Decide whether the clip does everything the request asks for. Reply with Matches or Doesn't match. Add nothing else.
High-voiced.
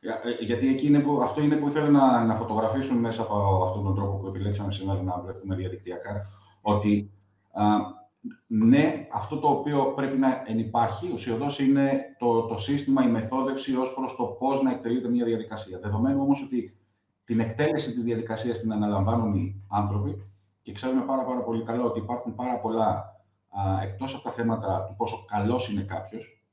Doesn't match